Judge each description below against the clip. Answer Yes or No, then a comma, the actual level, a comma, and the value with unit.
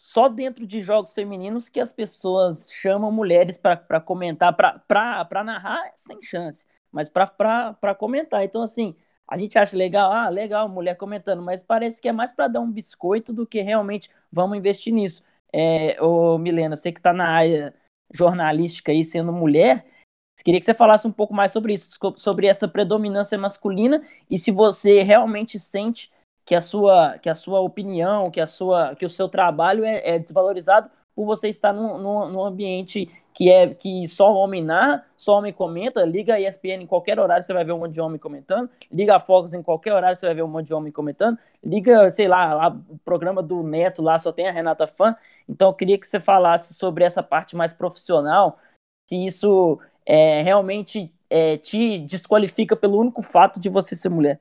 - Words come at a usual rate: No, fast, 195 wpm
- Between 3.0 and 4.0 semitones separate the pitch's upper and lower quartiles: Yes, average, 3.4 semitones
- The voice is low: No, high, 195 Hz